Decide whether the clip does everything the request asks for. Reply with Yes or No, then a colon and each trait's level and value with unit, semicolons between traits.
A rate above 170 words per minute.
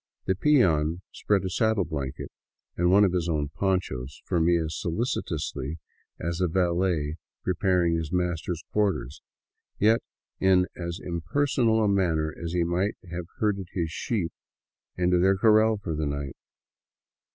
No: average, 150 wpm